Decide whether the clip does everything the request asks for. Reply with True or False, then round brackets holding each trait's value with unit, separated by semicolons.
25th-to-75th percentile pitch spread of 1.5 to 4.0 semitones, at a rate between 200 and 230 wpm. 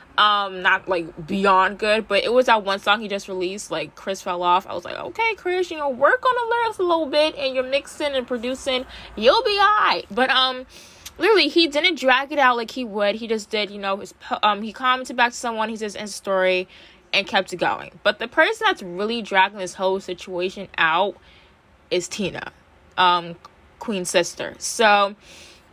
False (5.5 semitones; 205 wpm)